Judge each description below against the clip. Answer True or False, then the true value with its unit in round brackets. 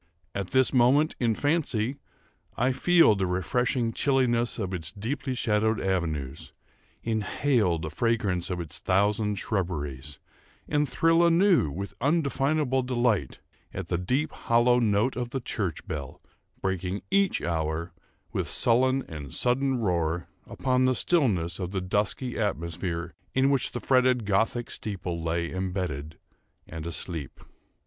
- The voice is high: False (105 Hz)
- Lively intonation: True (6.8 semitones)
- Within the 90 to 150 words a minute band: True (135 wpm)